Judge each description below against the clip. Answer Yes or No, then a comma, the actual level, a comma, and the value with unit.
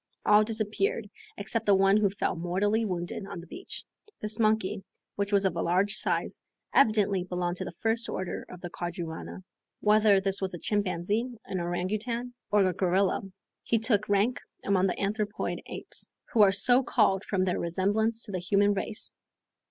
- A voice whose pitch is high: Yes, high, 200 Hz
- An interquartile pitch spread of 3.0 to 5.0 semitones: No, narrow, 2.6 semitones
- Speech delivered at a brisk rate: No, average, 170 wpm